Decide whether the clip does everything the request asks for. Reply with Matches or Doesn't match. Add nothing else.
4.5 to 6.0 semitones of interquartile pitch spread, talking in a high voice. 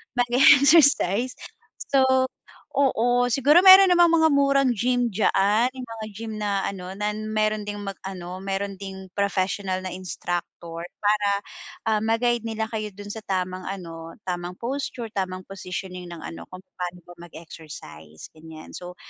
Matches